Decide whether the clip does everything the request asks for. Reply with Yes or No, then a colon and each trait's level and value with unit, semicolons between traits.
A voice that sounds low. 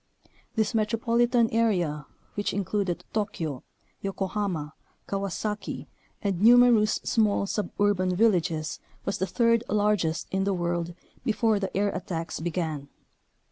No: high, 200 Hz